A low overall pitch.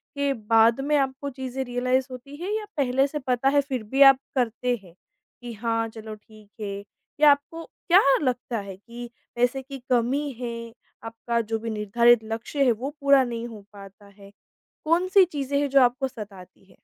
No: high, 245 Hz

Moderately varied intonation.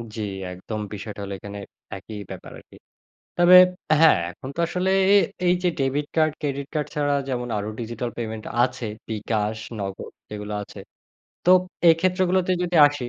No: wide, 7.3 semitones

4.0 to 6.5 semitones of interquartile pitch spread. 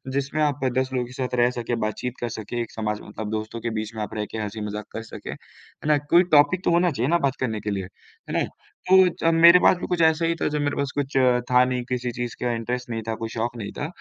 Yes: average, 4.7 semitones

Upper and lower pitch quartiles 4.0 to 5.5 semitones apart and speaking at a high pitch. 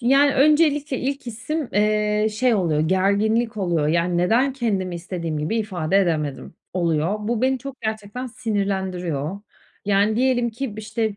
Yes: average, 5.2 semitones; high, 210 Hz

